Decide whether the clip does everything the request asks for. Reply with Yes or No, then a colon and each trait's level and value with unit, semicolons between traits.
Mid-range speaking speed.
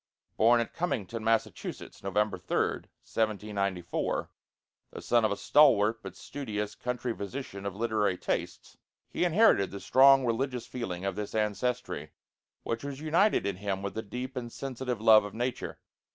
Yes: average, 150 wpm